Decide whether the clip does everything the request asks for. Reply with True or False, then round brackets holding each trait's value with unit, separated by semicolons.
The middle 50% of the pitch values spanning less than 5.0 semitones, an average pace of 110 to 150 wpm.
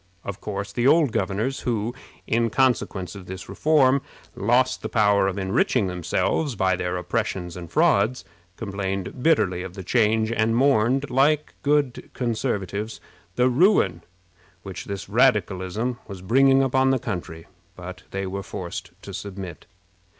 False (5.3 semitones; 145 wpm)